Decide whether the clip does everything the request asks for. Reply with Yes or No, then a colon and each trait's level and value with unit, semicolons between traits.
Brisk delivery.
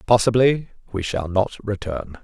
No: slow, 135 wpm